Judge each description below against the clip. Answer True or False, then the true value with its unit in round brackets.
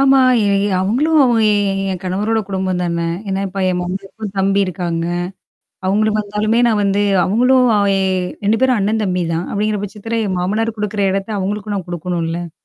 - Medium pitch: False (200 Hz)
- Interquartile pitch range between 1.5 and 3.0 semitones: True (2.7 semitones)